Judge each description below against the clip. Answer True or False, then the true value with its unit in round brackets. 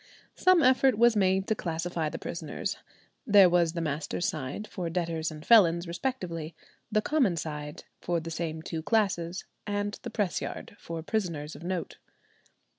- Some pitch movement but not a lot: True (4.2 semitones)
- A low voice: False (175 Hz)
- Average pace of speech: True (160 wpm)